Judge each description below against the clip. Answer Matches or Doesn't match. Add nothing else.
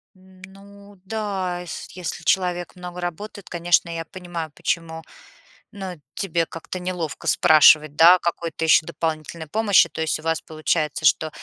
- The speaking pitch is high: Doesn't match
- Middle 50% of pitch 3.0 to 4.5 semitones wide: Doesn't match